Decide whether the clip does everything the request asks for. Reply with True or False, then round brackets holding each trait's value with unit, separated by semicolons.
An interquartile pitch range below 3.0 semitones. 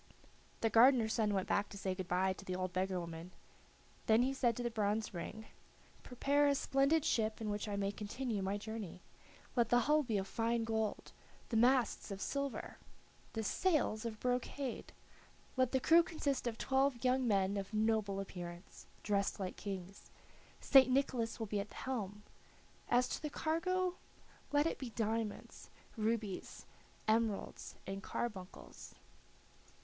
False (4.3 semitones)